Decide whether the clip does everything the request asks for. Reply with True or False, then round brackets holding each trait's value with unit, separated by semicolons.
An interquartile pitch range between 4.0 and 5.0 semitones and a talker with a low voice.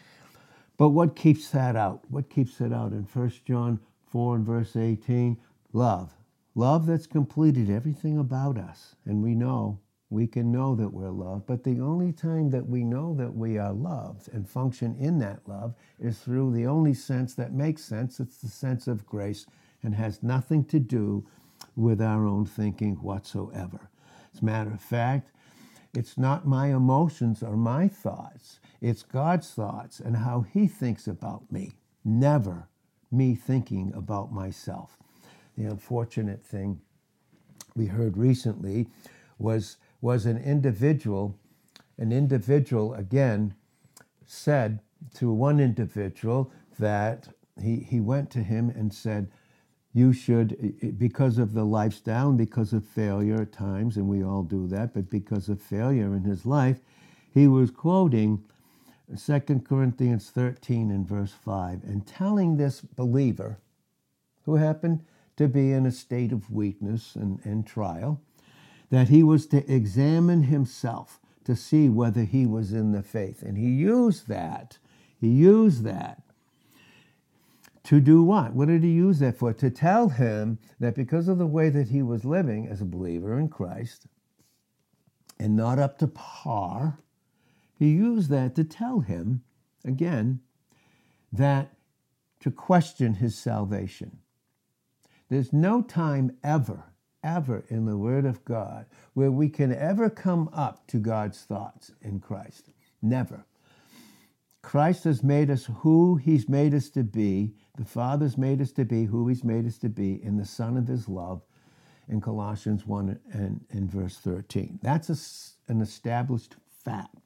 True (4.7 semitones; 120 Hz)